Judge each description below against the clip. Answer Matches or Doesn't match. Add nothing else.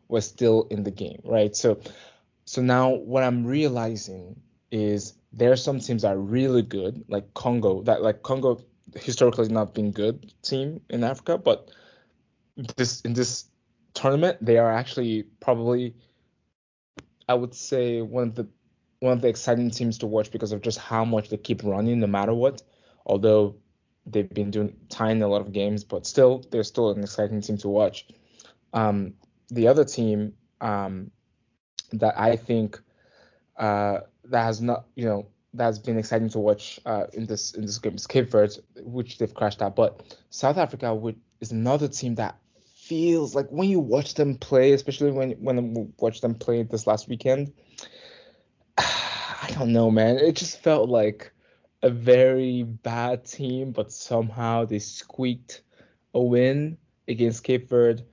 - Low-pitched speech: Matches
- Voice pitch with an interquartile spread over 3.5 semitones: Doesn't match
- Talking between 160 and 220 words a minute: Matches